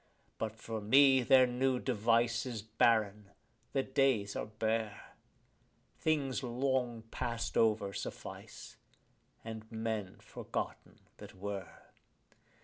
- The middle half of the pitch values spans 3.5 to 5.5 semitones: No, average, 3.0 semitones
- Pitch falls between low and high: No, low, 115 Hz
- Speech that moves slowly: Yes, slow, 105 wpm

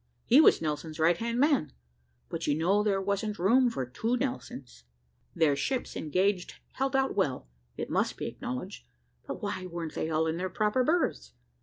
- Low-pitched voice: No, high, 190 Hz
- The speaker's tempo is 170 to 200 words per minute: Yes, average, 175 wpm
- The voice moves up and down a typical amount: No, wide, 7.1 semitones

